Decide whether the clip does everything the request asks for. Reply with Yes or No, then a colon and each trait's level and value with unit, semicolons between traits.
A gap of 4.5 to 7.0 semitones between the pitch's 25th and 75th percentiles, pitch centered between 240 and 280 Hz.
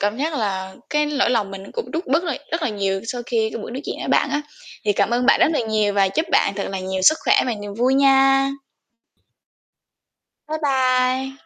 Yes: average, 5.1 semitones; very high, 250 Hz